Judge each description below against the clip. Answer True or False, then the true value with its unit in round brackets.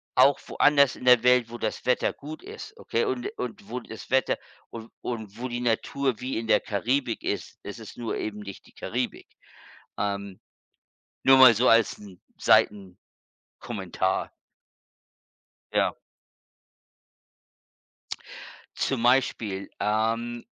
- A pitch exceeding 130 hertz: False (120 Hz)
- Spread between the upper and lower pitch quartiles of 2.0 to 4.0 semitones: True (2.6 semitones)